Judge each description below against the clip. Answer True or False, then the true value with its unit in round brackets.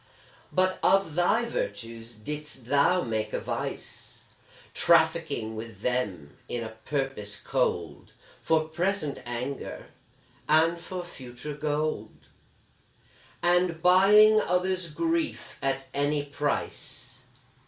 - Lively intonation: True (6.9 semitones)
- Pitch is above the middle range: False (145 Hz)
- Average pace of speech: False (100 wpm)